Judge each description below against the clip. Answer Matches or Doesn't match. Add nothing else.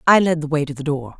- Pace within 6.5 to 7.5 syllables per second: Matches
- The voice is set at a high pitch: Doesn't match